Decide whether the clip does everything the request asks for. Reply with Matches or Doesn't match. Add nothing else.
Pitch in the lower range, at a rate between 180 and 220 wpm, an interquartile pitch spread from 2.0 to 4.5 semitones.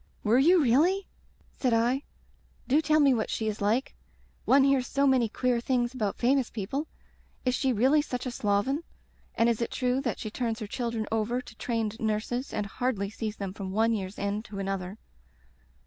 Doesn't match